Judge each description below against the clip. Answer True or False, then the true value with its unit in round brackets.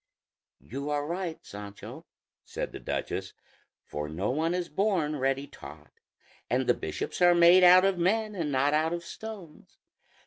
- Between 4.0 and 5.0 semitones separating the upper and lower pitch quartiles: True (4.3 semitones)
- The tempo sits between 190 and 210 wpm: False (160 wpm)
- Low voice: False (165 Hz)